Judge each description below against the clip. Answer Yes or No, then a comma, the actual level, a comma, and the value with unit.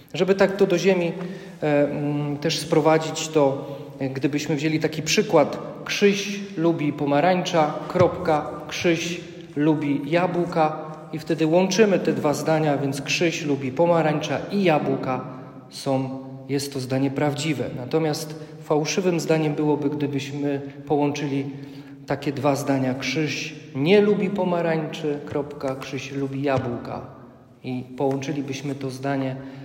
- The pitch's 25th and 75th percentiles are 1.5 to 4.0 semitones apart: Yes, average, 2.7 semitones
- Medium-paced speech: Yes, average, 120 wpm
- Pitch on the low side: No, medium, 150 Hz